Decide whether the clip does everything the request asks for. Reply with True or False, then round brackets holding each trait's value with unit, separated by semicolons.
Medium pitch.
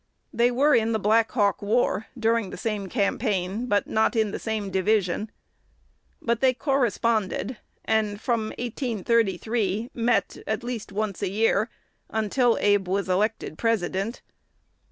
False (220 Hz)